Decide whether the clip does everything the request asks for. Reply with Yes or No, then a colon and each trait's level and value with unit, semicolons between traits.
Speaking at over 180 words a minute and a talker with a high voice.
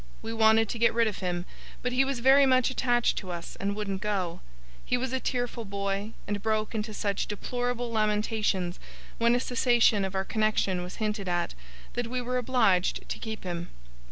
Yes: average, 190 wpm; high, 220 Hz